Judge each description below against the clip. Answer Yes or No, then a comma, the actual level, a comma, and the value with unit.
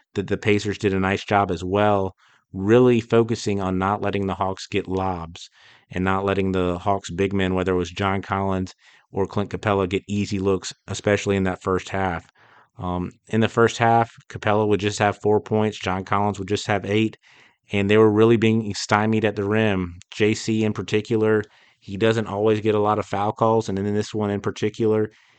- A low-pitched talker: Yes, low, 100 Hz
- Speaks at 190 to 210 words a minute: Yes, average, 200 wpm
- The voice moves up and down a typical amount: No, narrow, 2.0 semitones